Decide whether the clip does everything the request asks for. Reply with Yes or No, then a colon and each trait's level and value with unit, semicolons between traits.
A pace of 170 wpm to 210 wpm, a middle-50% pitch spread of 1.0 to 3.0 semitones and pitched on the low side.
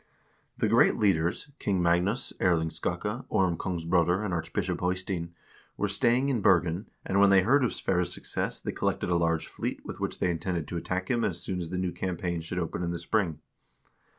Yes: fast, 205 wpm; narrow, 2.6 semitones; very low, 90 Hz